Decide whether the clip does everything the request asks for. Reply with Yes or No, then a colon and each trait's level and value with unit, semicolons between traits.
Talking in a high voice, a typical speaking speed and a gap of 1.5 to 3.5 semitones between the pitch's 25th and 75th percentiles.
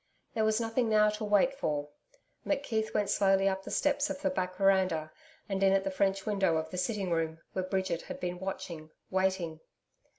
Yes: high, 195 Hz; average, 195 wpm; average, 2.9 semitones